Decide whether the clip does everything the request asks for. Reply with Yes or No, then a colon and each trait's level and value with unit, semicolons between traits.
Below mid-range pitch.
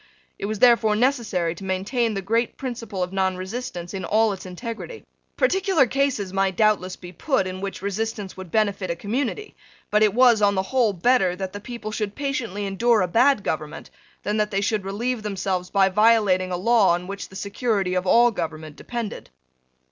No: high, 205 Hz